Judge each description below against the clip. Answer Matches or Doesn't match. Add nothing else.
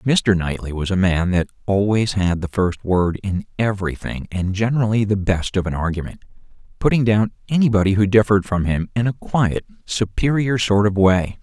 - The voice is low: Matches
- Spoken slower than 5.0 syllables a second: Doesn't match